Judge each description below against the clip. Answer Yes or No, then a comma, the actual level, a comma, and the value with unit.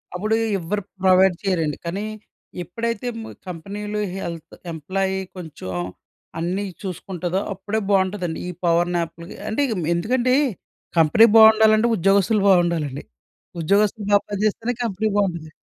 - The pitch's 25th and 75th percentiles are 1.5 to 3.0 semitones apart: No, average, 3.6 semitones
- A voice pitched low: No, high, 190 Hz